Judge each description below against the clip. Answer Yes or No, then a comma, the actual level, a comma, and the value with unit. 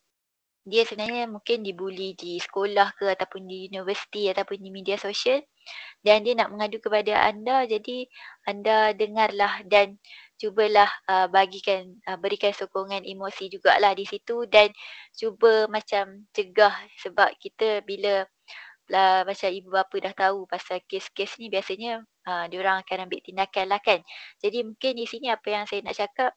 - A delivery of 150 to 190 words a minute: Yes, fast, 155 wpm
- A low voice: No, high, 200 Hz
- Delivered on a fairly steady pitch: Yes, narrow, 2.1 semitones